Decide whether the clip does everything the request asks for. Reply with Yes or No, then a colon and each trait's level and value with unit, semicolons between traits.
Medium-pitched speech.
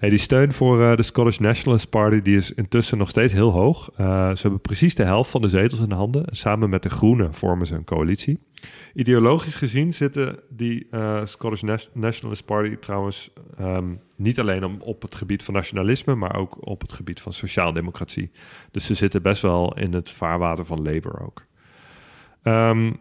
No: low, 105 Hz